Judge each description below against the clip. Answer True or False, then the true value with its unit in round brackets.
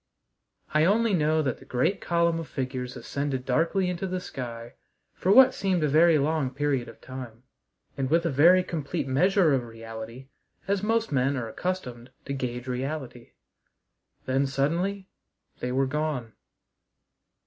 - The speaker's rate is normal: True (150 wpm)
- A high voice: False (140 Hz)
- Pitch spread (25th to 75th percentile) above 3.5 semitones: True (5.2 semitones)